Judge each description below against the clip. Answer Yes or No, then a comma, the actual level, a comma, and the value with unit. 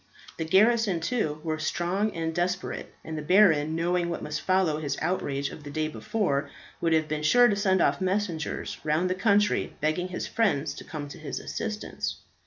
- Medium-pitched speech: Yes, medium, 170 Hz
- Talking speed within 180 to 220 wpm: Yes, average, 190 wpm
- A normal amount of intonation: Yes, average, 3.9 semitones